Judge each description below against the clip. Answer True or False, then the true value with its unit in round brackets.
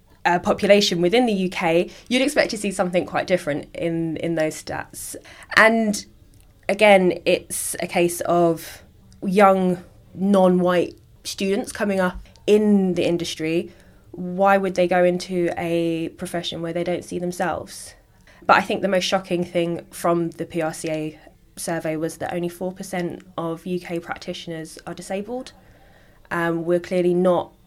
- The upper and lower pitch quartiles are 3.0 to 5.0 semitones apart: False (2.4 semitones)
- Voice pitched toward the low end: False (175 Hz)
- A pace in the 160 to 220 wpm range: False (145 wpm)